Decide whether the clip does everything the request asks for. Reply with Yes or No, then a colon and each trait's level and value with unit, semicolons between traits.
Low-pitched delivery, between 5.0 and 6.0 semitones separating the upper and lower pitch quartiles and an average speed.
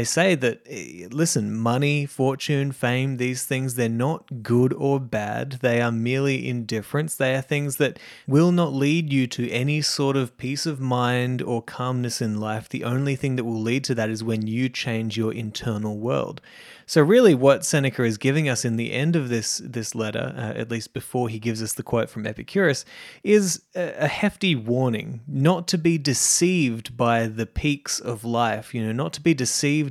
No: low, 125 Hz; average, 3.4 semitones; average, 195 wpm